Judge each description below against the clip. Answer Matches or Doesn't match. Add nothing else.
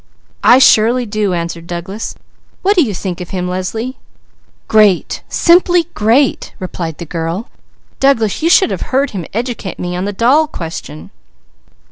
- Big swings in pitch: Matches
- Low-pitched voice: Doesn't match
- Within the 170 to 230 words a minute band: Doesn't match